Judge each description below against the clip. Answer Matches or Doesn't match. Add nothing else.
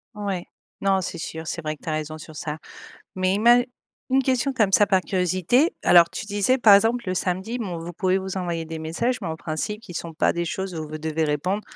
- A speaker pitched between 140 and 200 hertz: Matches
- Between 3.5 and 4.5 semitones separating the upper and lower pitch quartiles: Matches